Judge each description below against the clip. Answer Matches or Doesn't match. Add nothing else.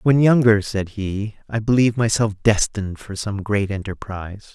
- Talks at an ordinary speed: Matches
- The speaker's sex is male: Matches